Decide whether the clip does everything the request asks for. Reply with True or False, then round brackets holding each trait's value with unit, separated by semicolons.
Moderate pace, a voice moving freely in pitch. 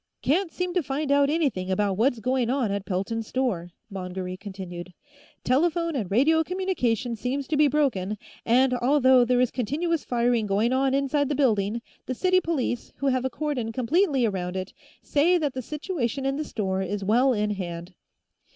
True (180 wpm; 5.7 semitones)